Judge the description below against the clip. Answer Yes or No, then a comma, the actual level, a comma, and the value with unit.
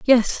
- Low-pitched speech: No, high, 240 Hz